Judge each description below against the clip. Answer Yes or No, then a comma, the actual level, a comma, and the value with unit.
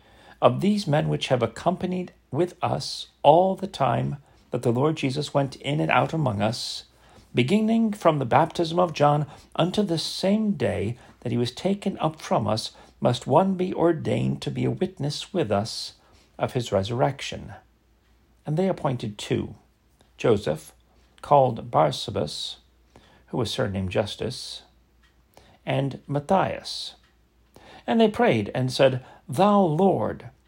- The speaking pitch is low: No, medium, 145 Hz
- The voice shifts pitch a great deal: Yes, wide, 7.8 semitones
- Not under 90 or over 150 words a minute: Yes, average, 140 wpm